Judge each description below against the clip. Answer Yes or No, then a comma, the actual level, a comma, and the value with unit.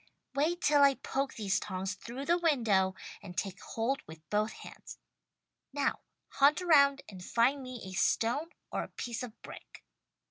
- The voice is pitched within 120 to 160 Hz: No, high, 245 Hz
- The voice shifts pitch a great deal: Yes, wide, 5.8 semitones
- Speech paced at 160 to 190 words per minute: Yes, average, 165 wpm